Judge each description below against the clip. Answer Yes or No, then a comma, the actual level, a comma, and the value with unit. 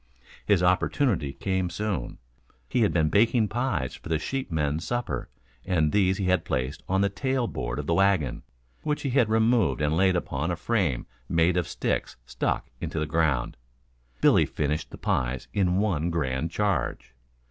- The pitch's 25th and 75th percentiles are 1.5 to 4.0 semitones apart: No, wide, 5.4 semitones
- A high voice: No, very low, 90 Hz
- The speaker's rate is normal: Yes, average, 170 wpm